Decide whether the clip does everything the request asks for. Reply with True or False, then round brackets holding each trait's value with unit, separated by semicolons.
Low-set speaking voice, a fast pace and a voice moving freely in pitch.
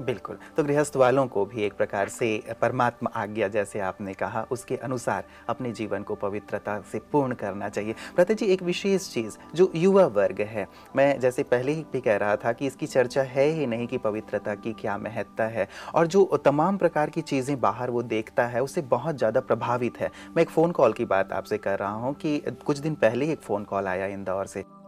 True (120 Hz; 210 wpm; 6.4 semitones)